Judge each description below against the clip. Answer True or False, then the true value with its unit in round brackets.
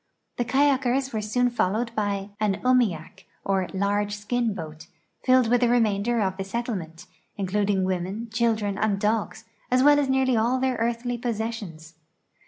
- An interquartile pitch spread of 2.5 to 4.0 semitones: True (3.7 semitones)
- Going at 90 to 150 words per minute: False (160 wpm)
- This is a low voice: False (220 Hz)